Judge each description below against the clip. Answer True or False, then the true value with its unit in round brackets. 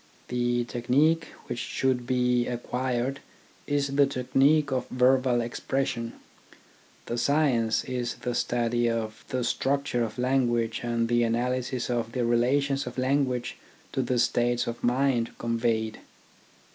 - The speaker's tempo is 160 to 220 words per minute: False (135 wpm)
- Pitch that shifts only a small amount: True (1.9 semitones)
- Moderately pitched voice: False (125 Hz)